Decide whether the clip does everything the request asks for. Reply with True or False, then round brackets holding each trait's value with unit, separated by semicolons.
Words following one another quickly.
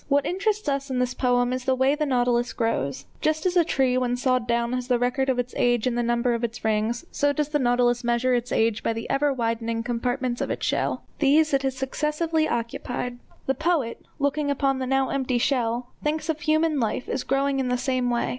True (225 wpm)